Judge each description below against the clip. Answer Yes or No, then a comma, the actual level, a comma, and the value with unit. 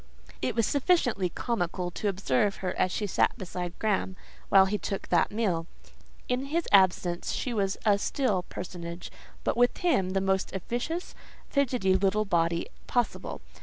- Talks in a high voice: Yes, high, 195 Hz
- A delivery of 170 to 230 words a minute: No, average, 155 wpm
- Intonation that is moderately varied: Yes, average, 4.4 semitones